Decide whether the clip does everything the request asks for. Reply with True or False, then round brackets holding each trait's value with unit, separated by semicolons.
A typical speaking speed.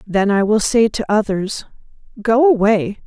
True (155 wpm)